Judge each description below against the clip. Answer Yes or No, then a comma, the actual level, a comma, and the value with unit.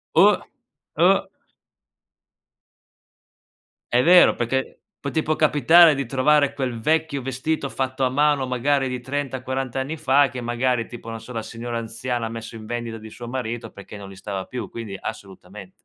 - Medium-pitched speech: No, low, 125 Hz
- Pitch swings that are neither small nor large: Yes, average, 3.3 semitones